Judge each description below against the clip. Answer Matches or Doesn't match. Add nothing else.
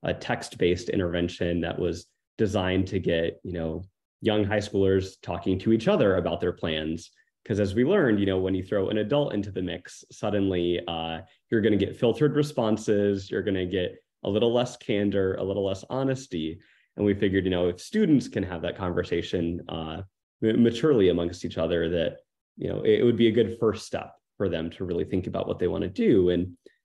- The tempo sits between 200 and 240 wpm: Matches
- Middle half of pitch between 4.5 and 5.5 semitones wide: Doesn't match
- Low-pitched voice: Matches